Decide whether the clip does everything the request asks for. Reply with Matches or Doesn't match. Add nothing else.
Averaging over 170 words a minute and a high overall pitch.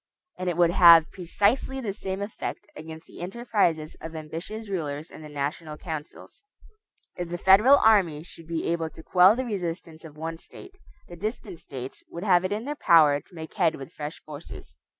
Doesn't match